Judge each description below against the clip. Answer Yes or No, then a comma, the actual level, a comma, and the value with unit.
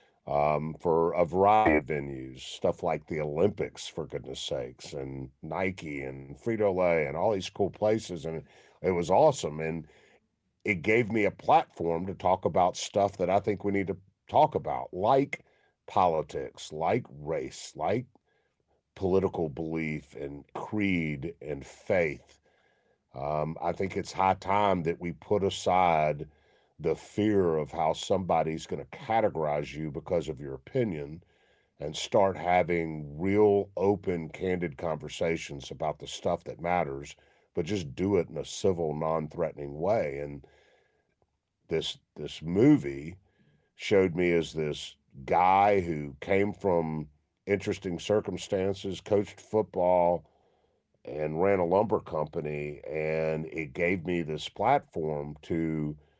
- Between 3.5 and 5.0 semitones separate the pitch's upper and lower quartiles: Yes, average, 4.2 semitones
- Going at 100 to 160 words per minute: Yes, slow, 135 wpm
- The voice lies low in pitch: Yes, very low, 85 Hz